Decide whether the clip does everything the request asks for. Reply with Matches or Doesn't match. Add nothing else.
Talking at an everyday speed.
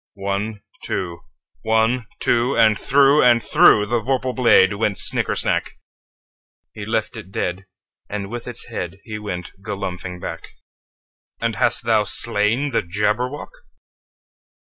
Doesn't match